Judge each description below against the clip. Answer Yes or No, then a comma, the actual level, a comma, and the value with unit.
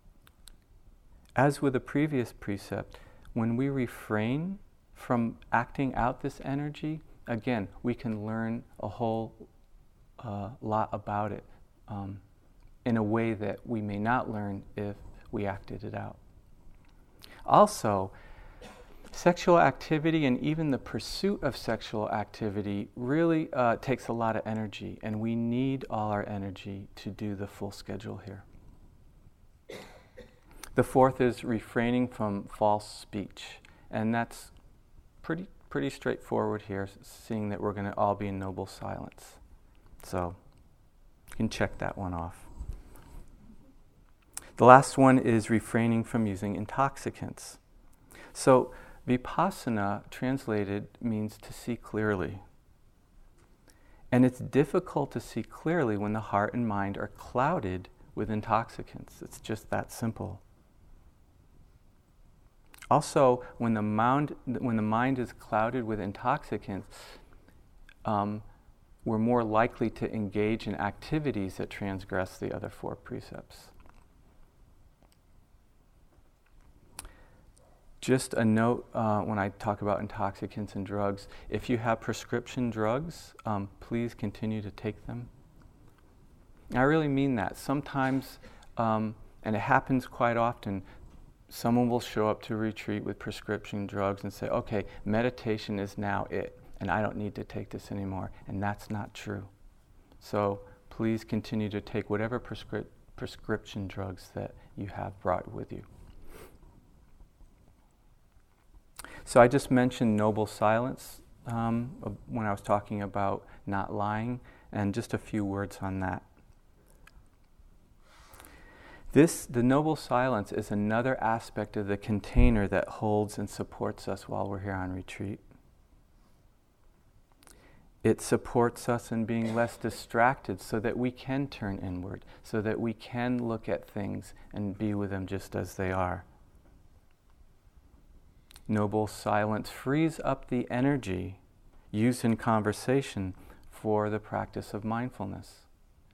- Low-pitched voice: Yes, low, 105 Hz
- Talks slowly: Yes, slow, 130 wpm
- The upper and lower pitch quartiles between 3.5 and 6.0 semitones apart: No, average, 3.0 semitones